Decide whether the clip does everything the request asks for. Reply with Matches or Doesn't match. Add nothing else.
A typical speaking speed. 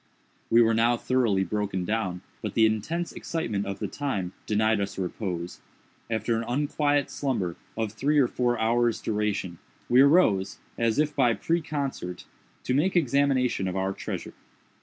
Matches